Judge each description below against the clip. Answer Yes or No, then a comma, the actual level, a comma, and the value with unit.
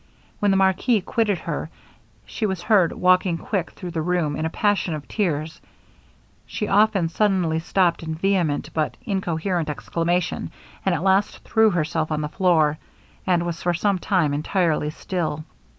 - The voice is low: No, medium, 175 Hz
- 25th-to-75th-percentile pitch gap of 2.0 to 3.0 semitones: No, average, 3.4 semitones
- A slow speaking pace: No, average, 160 wpm